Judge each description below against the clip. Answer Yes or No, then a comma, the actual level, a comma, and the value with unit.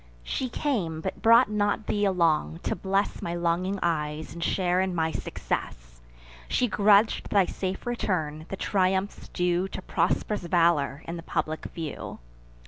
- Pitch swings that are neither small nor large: Yes, average, 3.6 semitones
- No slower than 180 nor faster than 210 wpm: No, average, 150 wpm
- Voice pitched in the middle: Yes, medium, 180 Hz